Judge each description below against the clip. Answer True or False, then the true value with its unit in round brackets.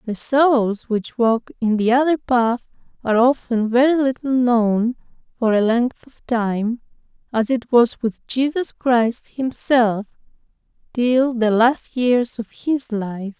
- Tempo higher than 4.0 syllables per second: False (3.6 syllables/s)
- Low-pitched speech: False (240 Hz)